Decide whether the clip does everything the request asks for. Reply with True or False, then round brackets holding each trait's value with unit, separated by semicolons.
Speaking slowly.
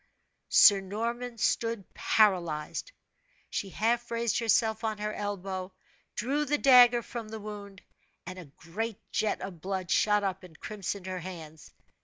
False (145 wpm)